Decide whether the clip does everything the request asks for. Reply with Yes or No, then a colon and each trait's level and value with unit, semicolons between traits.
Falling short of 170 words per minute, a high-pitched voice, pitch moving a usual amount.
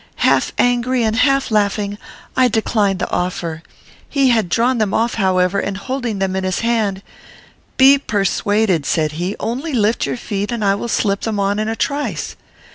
No: average, 180 wpm; high, 215 Hz; average, 3.5 semitones